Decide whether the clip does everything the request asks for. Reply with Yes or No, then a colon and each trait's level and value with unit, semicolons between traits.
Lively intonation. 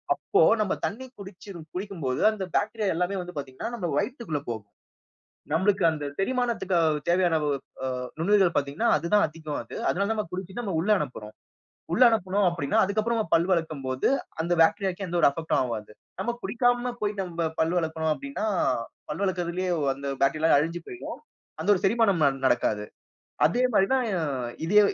No: average, 4.6 semitones